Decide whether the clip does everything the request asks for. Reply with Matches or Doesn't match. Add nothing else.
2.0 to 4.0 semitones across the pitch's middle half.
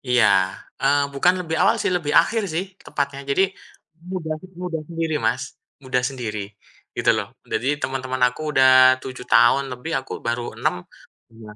Doesn't match